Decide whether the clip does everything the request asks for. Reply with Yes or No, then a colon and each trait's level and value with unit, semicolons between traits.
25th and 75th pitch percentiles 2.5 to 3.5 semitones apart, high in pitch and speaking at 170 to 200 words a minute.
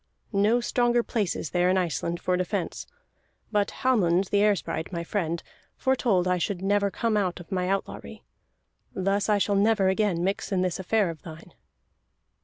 Yes: average, 2.8 semitones; high, 195 Hz; average, 175 wpm